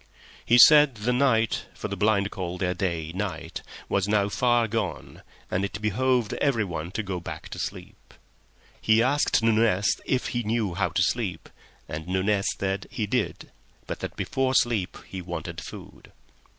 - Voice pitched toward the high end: No, low, 105 Hz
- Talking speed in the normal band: Yes, average, 155 wpm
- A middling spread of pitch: Yes, average, 4.1 semitones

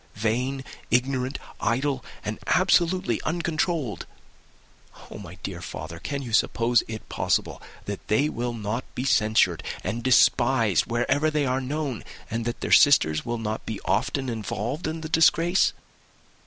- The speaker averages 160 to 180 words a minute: No, average, 140 wpm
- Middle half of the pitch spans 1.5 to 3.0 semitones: No, average, 4.4 semitones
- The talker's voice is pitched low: Yes, low, 125 Hz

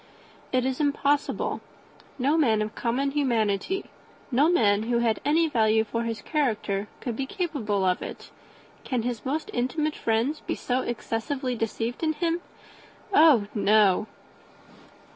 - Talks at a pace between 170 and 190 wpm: No, average, 140 wpm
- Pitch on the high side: Yes, high, 245 Hz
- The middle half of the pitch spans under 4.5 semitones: No, average, 4.9 semitones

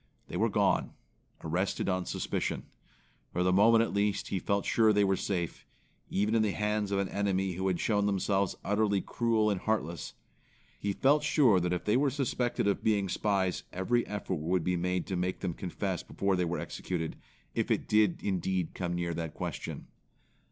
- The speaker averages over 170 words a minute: Yes, average, 185 wpm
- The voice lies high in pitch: No, very low, 95 Hz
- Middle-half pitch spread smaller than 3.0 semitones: Yes, narrow, 2.6 semitones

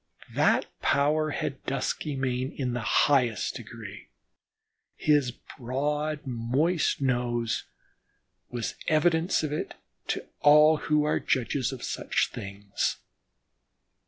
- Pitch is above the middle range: No, low, 135 Hz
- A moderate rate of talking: No, slow, 100 wpm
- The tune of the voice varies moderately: Yes, average, 3.6 semitones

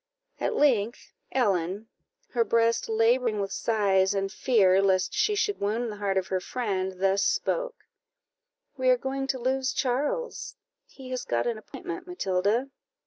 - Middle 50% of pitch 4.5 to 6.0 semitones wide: Yes, average, 5.1 semitones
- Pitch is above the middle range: Yes, high, 230 Hz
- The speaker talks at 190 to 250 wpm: No, average, 150 wpm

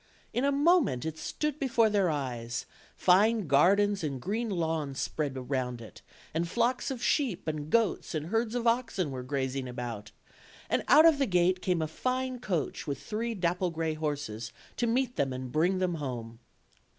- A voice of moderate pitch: Yes, medium, 170 Hz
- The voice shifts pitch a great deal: Yes, wide, 8.9 semitones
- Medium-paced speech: Yes, average, 180 wpm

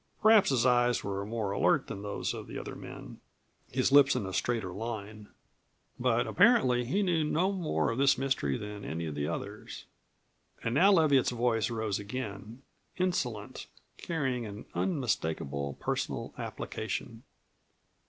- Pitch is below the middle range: Yes, low, 120 Hz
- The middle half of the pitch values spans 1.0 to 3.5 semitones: No, average, 5.1 semitones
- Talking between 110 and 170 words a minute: Yes, average, 145 wpm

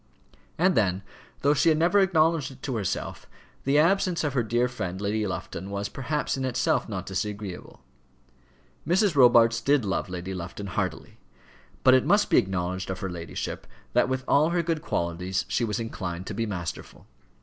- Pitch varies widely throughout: Yes, wide, 7.4 semitones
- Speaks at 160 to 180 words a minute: Yes, average, 175 wpm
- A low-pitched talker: Yes, low, 115 Hz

